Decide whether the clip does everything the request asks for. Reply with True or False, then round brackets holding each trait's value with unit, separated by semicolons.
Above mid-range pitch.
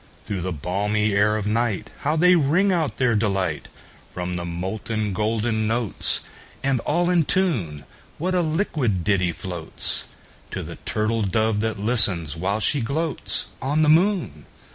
False (110 Hz)